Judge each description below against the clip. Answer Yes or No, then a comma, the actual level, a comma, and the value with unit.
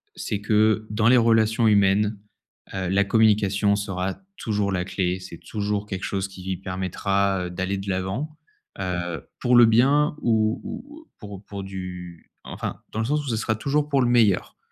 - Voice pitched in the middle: No, low, 105 Hz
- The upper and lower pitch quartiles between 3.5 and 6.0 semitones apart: No, average, 2.9 semitones